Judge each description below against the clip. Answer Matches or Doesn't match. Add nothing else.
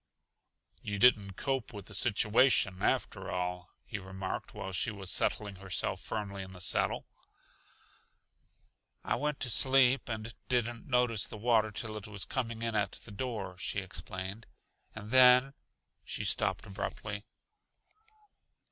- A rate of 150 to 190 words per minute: Doesn't match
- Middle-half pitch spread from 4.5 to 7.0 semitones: Doesn't match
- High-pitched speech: Doesn't match